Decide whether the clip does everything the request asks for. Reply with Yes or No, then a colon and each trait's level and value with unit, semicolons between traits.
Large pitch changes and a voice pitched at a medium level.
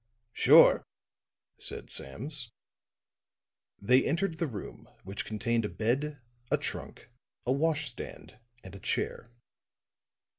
No: wide, 5.7 semitones; low, 125 Hz